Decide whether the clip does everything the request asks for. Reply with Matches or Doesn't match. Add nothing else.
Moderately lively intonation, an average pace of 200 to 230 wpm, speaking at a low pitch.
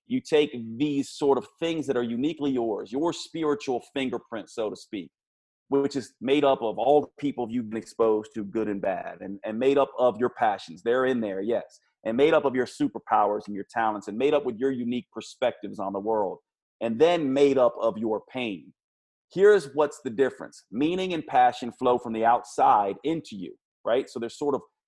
Matches